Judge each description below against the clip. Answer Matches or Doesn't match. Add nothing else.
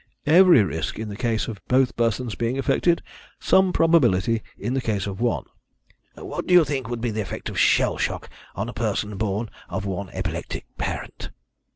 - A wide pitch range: Doesn't match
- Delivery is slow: Doesn't match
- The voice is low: Matches